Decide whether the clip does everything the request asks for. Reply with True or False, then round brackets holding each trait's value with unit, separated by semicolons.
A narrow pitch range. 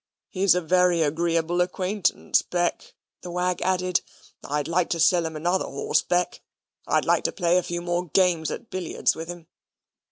True (1.5 semitones)